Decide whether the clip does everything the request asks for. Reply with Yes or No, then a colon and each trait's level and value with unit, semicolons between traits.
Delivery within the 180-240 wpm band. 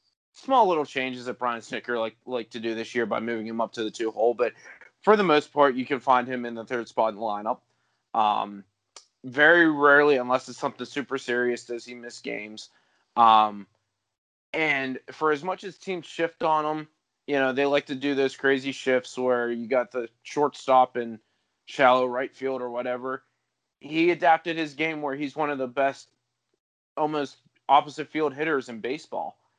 Yes: average, 190 wpm